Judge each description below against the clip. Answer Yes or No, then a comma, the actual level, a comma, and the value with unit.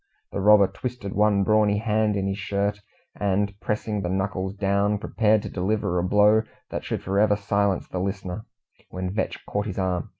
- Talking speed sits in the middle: Yes, average, 180 wpm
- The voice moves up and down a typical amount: No, narrow, 1.6 semitones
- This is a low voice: Yes, low, 100 Hz